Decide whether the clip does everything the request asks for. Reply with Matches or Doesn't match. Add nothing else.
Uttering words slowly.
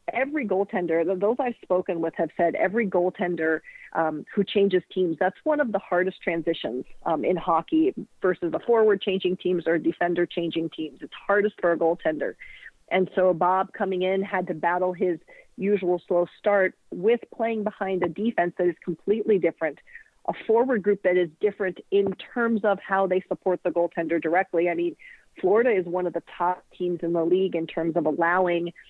Doesn't match